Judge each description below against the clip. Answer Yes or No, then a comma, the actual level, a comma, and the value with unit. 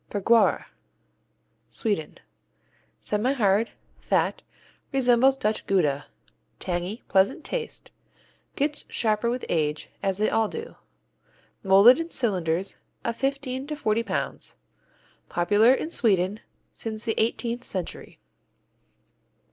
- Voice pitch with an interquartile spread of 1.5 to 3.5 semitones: No, average, 4.8 semitones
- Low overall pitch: No, high, 220 Hz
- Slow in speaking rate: Yes, slow, 100 wpm